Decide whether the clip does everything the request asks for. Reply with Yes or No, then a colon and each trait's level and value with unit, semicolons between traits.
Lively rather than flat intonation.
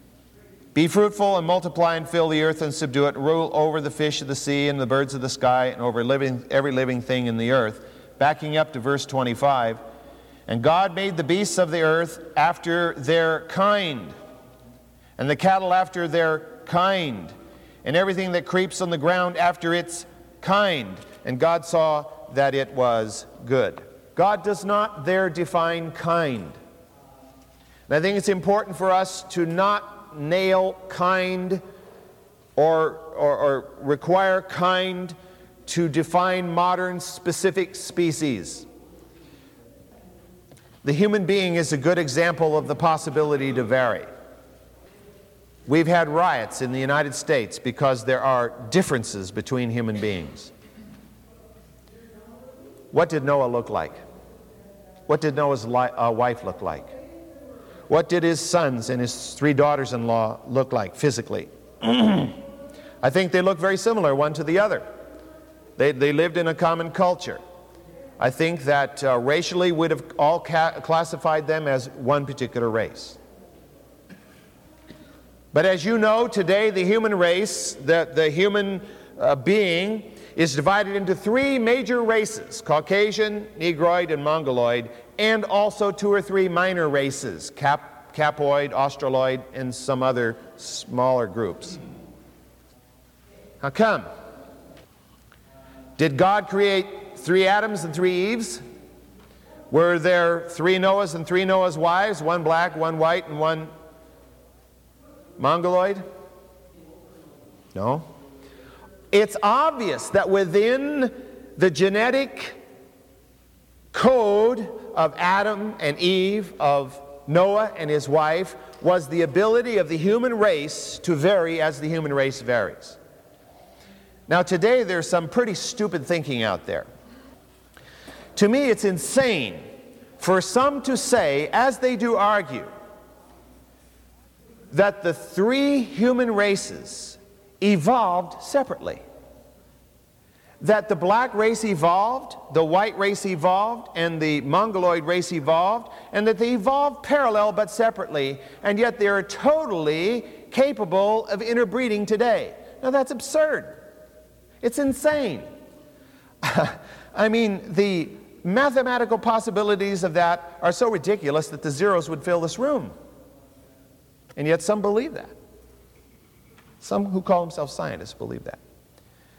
Yes: wide, 5.7 semitones